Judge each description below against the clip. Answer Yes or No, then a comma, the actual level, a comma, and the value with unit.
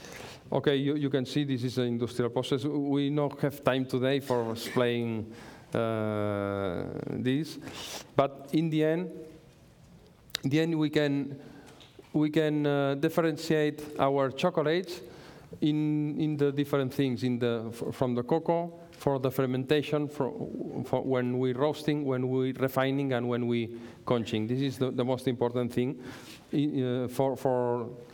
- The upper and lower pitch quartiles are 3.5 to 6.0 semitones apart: No, average, 3.1 semitones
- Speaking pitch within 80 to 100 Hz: No, low, 135 Hz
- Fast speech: No, average, 155 wpm